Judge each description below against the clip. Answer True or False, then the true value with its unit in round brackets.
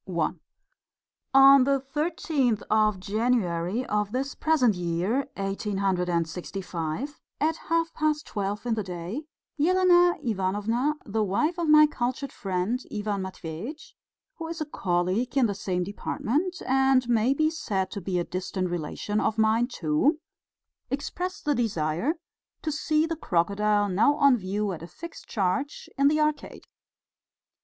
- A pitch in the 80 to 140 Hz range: False (225 Hz)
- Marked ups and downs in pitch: True (7.5 semitones)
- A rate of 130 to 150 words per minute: True (140 wpm)